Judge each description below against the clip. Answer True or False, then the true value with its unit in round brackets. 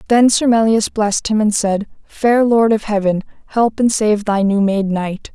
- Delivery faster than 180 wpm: True (200 wpm)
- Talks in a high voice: True (215 Hz)